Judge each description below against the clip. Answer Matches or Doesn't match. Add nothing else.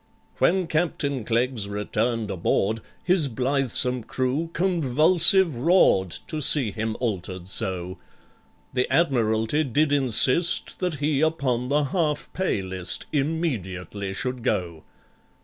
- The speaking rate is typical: Doesn't match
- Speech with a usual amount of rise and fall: Doesn't match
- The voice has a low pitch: Matches